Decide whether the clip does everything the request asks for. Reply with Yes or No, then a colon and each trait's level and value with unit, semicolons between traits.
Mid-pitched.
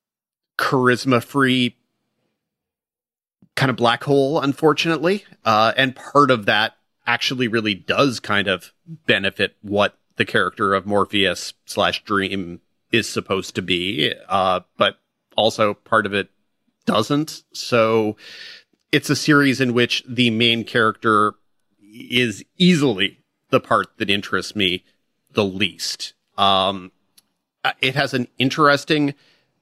No: low, 120 Hz